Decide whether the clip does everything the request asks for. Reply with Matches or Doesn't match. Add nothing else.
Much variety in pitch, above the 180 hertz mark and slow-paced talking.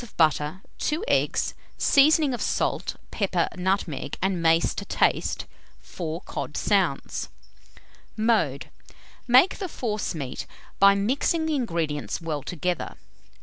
Matches